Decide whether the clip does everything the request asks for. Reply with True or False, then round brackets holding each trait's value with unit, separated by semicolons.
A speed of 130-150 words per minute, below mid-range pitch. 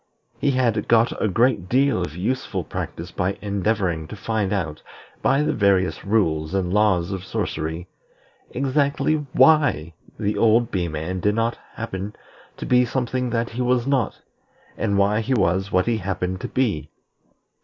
False (160 wpm; 105 Hz)